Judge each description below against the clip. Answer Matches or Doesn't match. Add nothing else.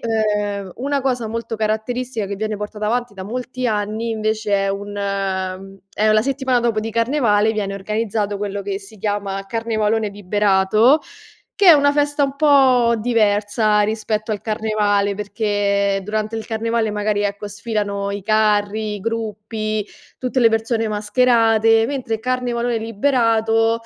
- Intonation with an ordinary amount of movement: Doesn't match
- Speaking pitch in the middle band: Doesn't match